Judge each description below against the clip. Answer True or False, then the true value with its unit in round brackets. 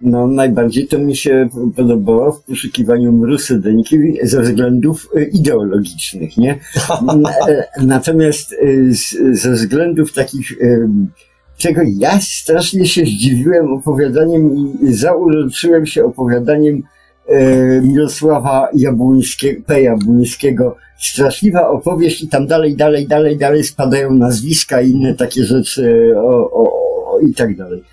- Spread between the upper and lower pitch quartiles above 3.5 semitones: True (4.2 semitones)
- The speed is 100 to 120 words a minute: True (110 wpm)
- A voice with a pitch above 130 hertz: True (140 Hz)